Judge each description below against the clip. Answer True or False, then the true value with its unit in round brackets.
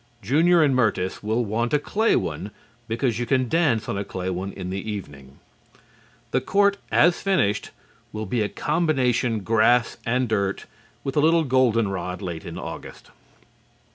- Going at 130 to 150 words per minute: False (165 wpm)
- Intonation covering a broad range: True (6.0 semitones)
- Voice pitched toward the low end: True (115 Hz)